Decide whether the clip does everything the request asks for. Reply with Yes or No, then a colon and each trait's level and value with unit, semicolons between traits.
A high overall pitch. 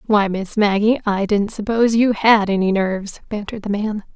Yes: high, 210 Hz